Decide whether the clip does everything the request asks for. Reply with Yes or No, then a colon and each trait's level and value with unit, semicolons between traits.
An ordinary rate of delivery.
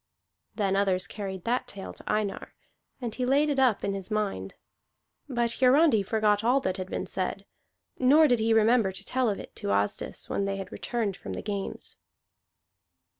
Yes: average, 180 wpm